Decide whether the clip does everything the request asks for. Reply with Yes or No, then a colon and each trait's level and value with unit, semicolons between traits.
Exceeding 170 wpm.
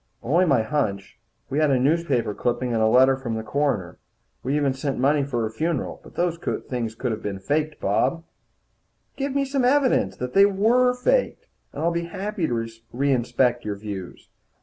Yes: average, 185 wpm